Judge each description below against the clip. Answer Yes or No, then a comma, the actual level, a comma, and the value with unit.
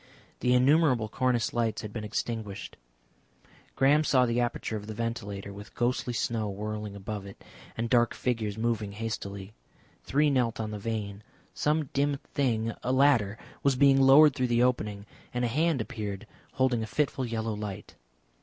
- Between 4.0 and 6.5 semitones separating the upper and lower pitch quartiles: No, average, 3.3 semitones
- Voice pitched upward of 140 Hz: No, low, 115 Hz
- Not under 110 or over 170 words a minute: Yes, average, 165 wpm